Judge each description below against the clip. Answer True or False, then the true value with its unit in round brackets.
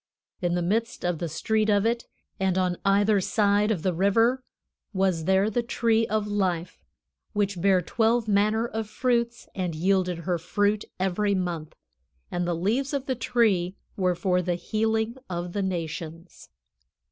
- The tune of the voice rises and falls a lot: False (3.7 semitones)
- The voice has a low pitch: False (195 Hz)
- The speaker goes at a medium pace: True (160 wpm)